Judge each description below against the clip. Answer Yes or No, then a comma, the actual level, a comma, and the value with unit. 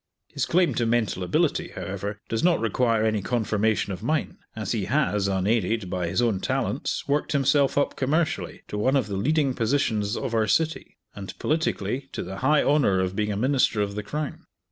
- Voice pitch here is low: Yes, low, 110 Hz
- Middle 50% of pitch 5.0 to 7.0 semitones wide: Yes, wide, 5.4 semitones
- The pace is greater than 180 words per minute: Yes, average, 190 wpm